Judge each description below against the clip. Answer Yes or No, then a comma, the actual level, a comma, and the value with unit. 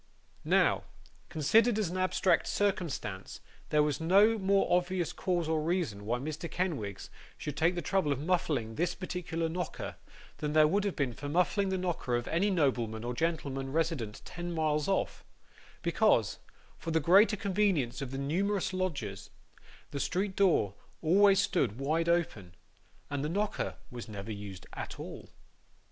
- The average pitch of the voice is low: No, medium, 165 Hz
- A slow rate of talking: No, average, 160 wpm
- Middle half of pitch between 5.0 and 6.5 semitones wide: Yes, wide, 5.4 semitones